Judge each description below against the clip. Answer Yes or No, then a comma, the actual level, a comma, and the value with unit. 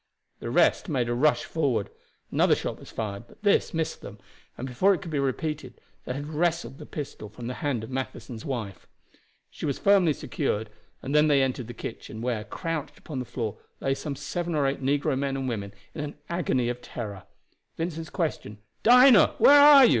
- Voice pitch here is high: No, low, 135 Hz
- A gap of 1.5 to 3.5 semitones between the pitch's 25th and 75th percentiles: No, average, 4.9 semitones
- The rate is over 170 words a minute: Yes, average, 200 wpm